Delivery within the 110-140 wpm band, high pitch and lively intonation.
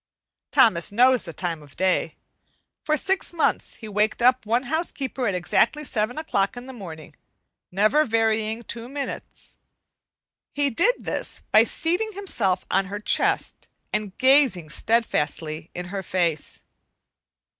Yes: slow, 135 wpm; high, 225 Hz; wide, 6.2 semitones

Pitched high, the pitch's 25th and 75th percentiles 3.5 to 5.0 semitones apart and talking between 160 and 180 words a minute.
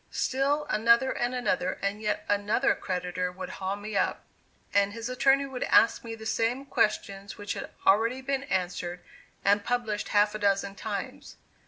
Yes: high, 210 Hz; average, 3.8 semitones; average, 165 wpm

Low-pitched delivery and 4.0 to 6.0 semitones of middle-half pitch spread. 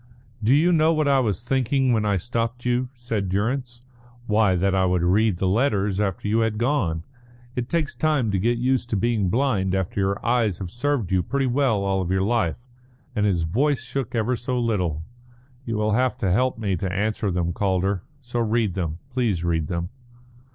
Yes: low, 110 Hz; average, 4.6 semitones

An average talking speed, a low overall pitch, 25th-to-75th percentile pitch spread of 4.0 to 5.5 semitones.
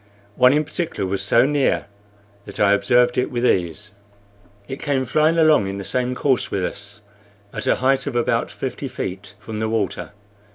Yes: average, 180 wpm; low, 120 Hz; average, 4.8 semitones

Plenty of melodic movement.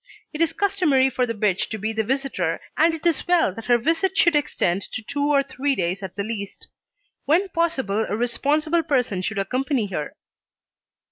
Yes: wide, 6.8 semitones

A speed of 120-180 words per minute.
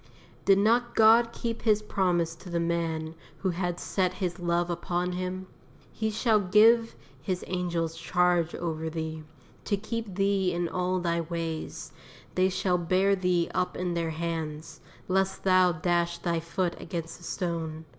Yes: average, 155 wpm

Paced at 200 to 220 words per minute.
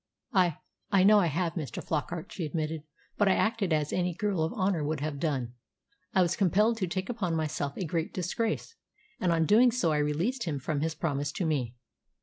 Yes: fast, 205 wpm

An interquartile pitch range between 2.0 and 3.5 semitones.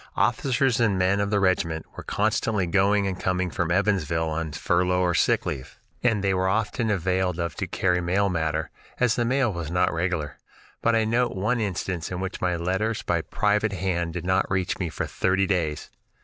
Yes: average, 3.1 semitones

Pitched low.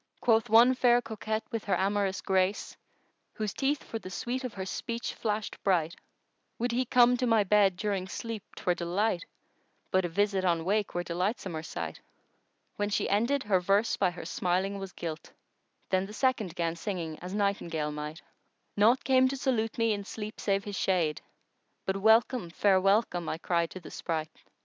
No: high, 200 Hz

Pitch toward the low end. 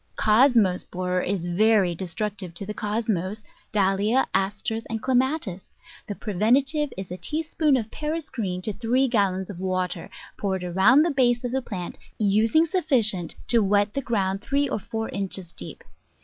No: high, 210 Hz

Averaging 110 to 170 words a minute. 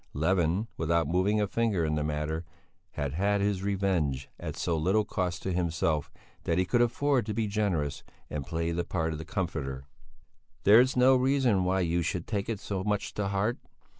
No: average, 190 wpm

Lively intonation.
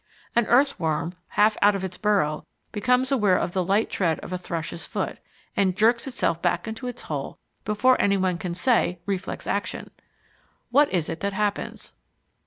No: average, 4.2 semitones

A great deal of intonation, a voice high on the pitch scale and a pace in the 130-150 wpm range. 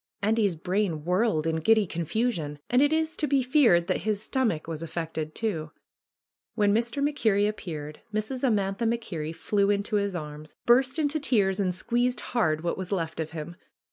No: wide, 6.3 semitones; high, 200 Hz; average, 175 wpm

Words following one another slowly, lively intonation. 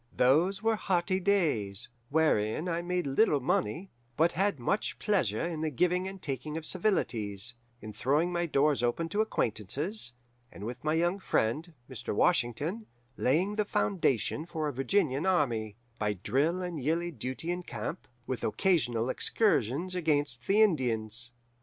No: average, 150 wpm; wide, 6.8 semitones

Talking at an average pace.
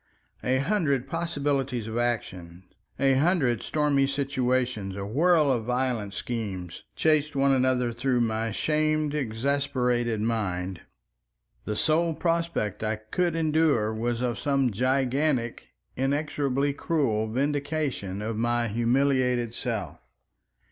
No: slow, 115 wpm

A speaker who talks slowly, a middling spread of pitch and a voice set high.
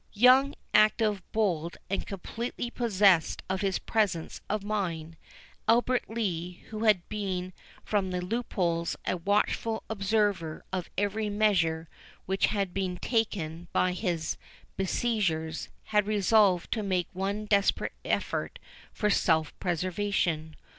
Yes: slow, 120 wpm; average, 3.4 semitones; high, 195 Hz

